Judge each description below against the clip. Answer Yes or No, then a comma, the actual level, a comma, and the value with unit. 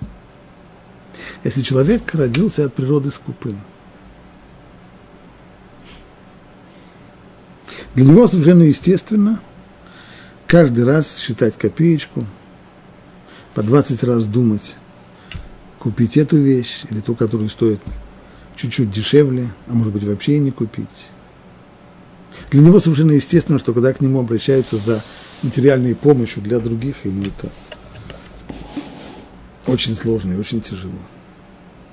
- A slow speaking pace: Yes, slow, 105 wpm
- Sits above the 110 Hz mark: Yes, low, 125 Hz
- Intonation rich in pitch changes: No, average, 4.7 semitones